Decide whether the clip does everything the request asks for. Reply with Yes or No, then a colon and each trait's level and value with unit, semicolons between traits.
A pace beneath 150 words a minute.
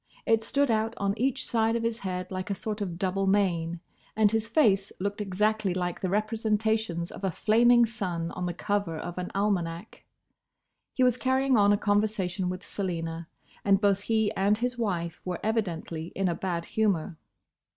No: average, 180 wpm